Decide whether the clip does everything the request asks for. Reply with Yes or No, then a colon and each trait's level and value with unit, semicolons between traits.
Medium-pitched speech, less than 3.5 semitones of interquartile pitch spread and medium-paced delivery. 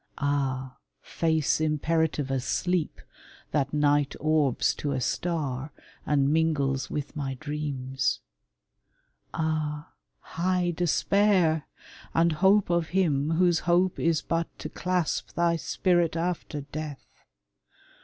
No: medium, 155 Hz; average, 3.0 semitones; slow, 110 wpm